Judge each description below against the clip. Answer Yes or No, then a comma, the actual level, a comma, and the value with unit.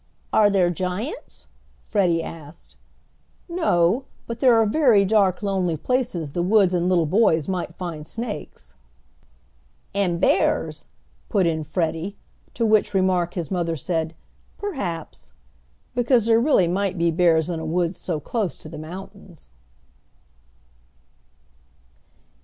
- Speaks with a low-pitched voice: No, medium, 180 Hz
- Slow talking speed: Yes, slow, 125 wpm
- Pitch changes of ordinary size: Yes, average, 4.3 semitones